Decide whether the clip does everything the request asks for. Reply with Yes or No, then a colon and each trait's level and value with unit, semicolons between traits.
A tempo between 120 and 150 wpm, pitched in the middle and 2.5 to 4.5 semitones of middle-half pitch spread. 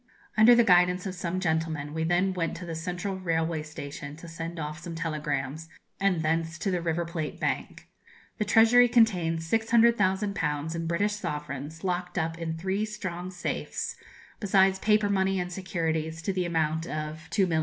No: average, 165 wpm; medium, 170 Hz; average, 3.0 semitones